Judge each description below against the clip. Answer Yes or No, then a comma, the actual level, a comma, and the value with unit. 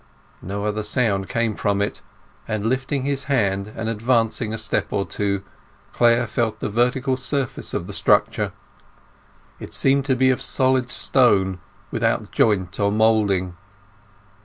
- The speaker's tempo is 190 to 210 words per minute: No, average, 145 wpm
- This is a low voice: Yes, low, 110 Hz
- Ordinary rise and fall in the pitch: Yes, average, 4.0 semitones